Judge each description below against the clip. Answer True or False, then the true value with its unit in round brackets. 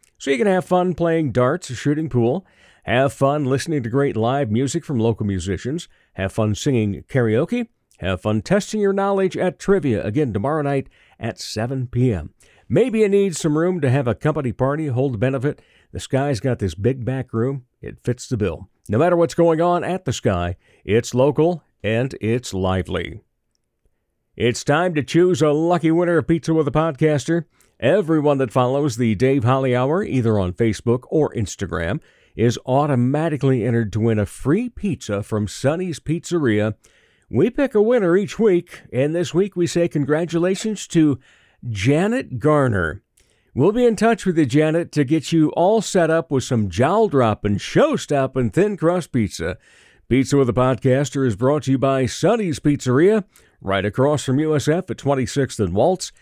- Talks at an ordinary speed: True (175 wpm)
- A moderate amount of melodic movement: False (5.8 semitones)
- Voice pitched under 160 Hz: True (140 Hz)